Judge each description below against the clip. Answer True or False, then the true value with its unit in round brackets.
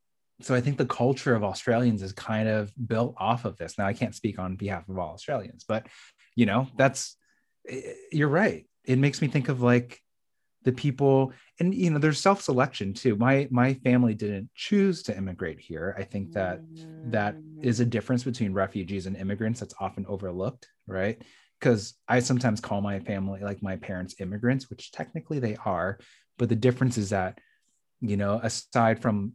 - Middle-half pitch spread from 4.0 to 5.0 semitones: True (4.4 semitones)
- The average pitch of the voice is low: True (115 Hz)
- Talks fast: False (185 wpm)